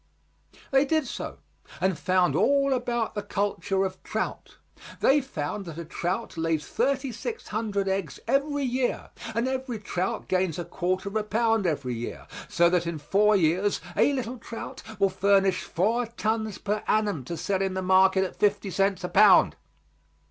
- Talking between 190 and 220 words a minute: No, average, 170 wpm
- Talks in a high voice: Yes, high, 200 Hz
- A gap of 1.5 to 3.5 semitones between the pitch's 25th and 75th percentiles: No, average, 4.0 semitones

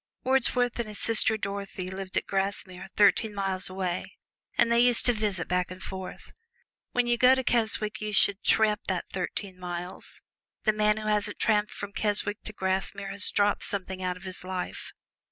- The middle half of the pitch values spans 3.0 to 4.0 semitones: No, narrow, 2.4 semitones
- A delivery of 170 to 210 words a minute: Yes, average, 180 wpm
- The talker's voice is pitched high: Yes, high, 200 Hz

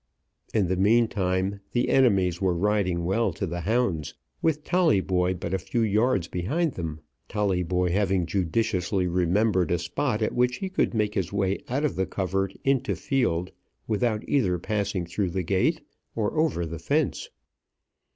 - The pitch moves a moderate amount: Yes, average, 4.1 semitones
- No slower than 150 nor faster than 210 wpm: Yes, average, 160 wpm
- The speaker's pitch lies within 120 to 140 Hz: No, very low, 95 Hz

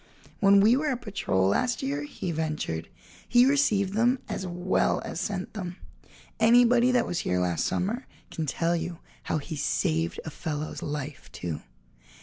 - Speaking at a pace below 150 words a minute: No, average, 160 wpm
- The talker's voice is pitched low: No, medium, 175 Hz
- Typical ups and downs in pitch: No, wide, 7.3 semitones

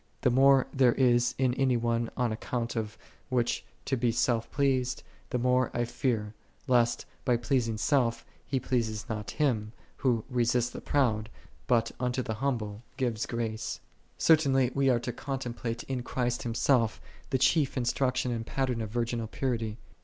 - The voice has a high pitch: No, low, 120 Hz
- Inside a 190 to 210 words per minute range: No, average, 165 wpm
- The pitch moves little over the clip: Yes, narrow, 2.1 semitones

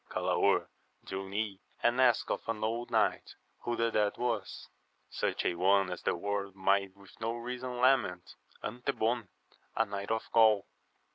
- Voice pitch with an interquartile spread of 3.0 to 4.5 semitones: Yes, average, 3.3 semitones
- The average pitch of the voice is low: Yes, low, 110 Hz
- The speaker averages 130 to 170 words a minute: Yes, average, 155 wpm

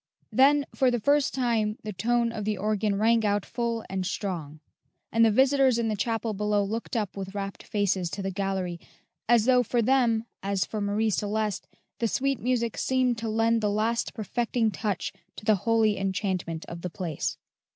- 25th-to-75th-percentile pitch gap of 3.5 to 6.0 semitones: No, average, 2.9 semitones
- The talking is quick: No, average, 185 wpm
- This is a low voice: No, high, 215 Hz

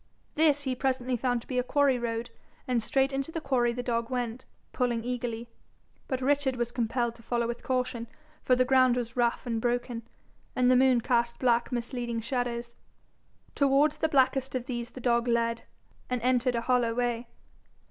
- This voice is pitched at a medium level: No, high, 245 Hz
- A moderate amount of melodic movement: No, narrow, 1.6 semitones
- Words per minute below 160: No, average, 180 wpm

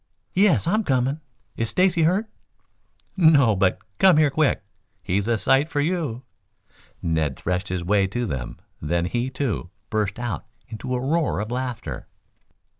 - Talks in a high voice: No, low, 125 Hz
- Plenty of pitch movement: Yes, wide, 7.6 semitones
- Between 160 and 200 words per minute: No, average, 150 wpm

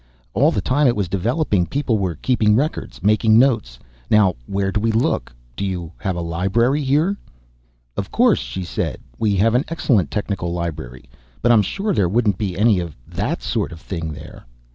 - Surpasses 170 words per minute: Yes, average, 185 wpm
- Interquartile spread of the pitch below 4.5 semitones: No, wide, 5.4 semitones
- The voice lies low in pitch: Yes, low, 100 Hz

